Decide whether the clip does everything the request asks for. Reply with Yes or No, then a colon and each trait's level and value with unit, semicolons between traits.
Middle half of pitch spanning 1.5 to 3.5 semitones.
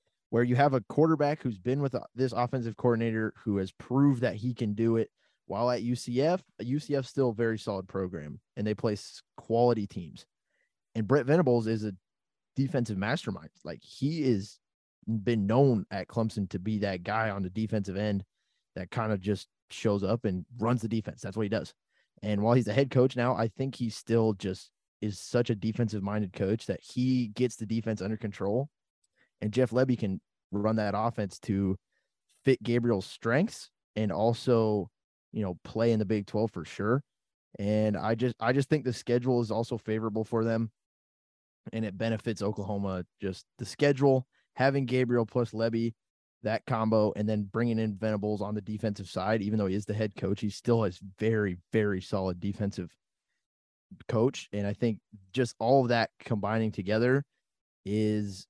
Yes: average, 2.9 semitones